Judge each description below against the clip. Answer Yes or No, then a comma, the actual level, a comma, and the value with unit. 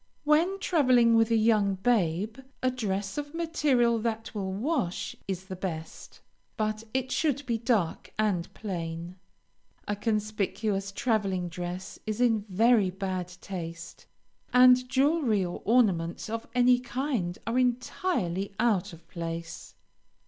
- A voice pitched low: No, high, 215 Hz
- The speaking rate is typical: No, slow, 130 wpm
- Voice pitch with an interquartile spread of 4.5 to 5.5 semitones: Yes, average, 4.9 semitones